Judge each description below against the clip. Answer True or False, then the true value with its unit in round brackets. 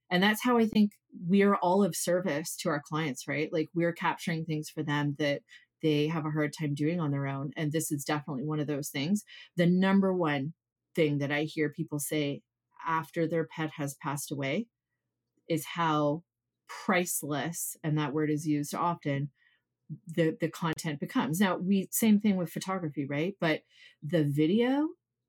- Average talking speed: True (180 wpm)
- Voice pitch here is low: False (160 Hz)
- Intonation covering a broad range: False (3.0 semitones)